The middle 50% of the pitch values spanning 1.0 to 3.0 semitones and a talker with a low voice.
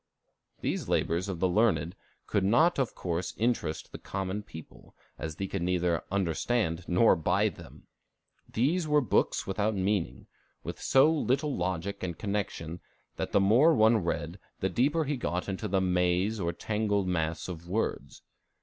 No: average, 4.2 semitones; very low, 95 Hz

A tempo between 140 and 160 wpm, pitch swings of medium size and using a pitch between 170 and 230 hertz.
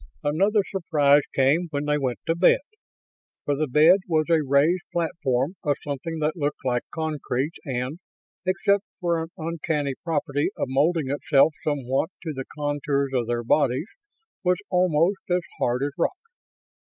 No: average, 155 wpm; average, 3.3 semitones; medium, 150 Hz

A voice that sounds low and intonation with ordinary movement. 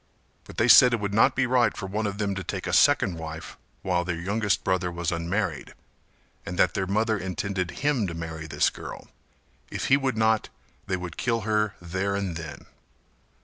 Yes: low, 100 Hz; average, 3.9 semitones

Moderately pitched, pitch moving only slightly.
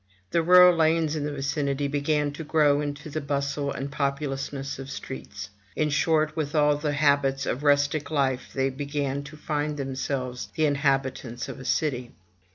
Yes: medium, 145 Hz; narrow, 1.8 semitones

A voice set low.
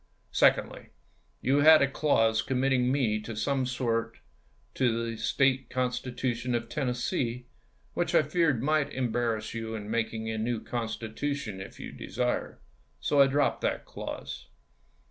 Yes: low, 125 Hz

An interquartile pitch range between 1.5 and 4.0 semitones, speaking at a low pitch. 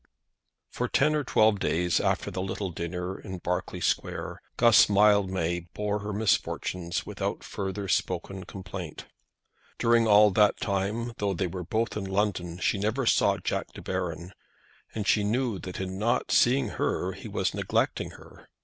Yes: narrow, 2.6 semitones; low, 100 Hz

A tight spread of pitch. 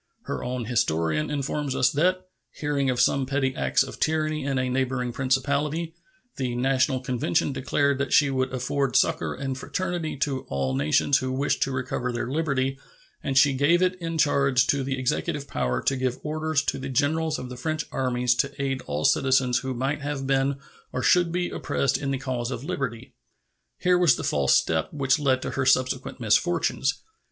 Yes: narrow, 2.3 semitones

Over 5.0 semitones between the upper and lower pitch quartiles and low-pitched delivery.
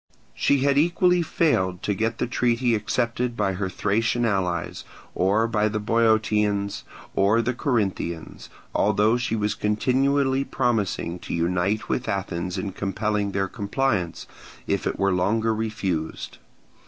No: average, 3.5 semitones; low, 105 Hz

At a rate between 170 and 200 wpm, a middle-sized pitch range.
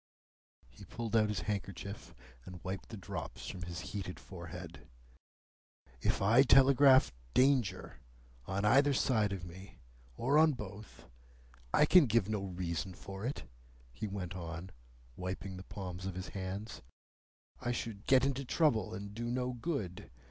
No: average, 150 wpm; average, 4.8 semitones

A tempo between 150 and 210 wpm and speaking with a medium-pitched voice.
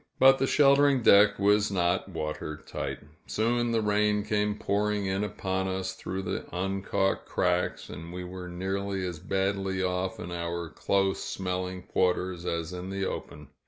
No: average, 160 wpm; very low, 95 Hz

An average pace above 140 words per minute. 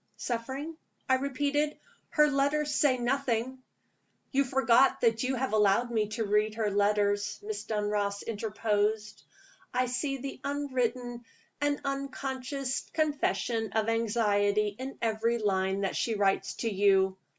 No: slow, 135 wpm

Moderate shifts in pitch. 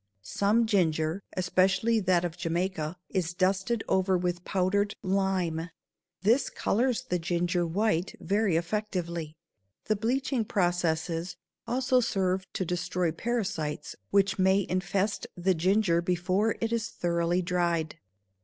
Yes: average, 3.0 semitones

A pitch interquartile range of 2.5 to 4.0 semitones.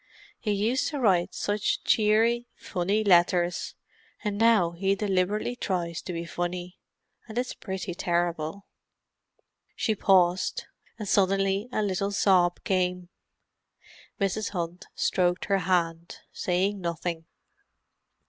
Yes: average, 2.9 semitones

